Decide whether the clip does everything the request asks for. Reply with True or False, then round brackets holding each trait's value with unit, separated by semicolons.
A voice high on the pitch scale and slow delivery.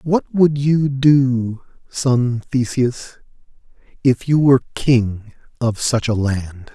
False (125 Hz; 125 wpm)